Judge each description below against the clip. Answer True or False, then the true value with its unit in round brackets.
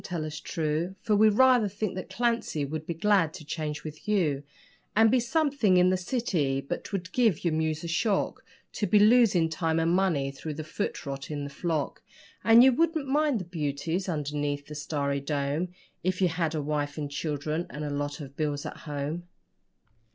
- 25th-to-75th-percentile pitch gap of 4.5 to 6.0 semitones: True (5.5 semitones)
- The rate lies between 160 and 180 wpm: False (195 wpm)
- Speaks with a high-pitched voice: False (165 Hz)